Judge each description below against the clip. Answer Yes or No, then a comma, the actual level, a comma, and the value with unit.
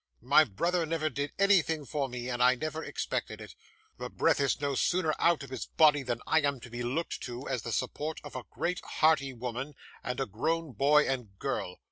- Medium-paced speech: No, fast, 210 wpm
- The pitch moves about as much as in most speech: Yes, average, 4.0 semitones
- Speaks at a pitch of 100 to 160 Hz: Yes, medium, 140 Hz